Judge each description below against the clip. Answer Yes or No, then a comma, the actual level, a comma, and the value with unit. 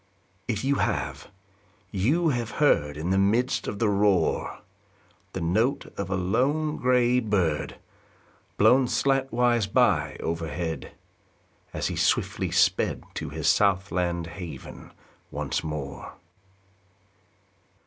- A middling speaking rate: No, slow, 115 wpm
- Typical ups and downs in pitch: No, wide, 6.4 semitones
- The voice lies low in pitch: Yes, low, 100 Hz